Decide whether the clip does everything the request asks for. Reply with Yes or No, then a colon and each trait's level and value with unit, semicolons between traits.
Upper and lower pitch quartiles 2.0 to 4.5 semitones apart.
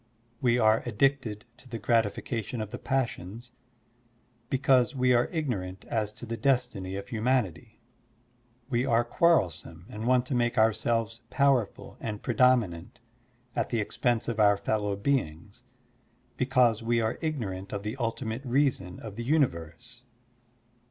Yes: average, 3.5 semitones